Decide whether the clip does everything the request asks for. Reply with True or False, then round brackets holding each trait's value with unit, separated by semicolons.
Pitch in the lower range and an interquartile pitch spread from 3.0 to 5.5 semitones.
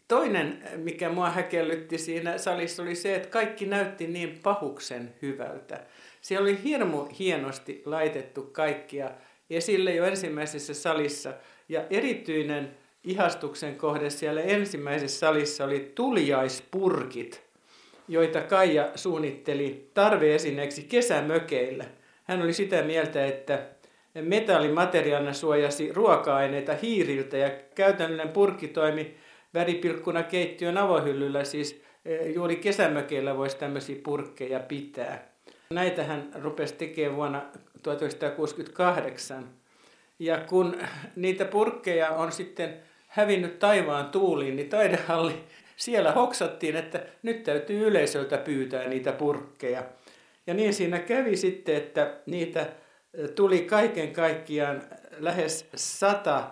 False (160 Hz; 3.8 semitones)